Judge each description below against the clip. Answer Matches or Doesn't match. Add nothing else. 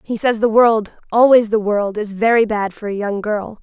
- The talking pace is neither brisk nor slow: Doesn't match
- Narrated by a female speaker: Matches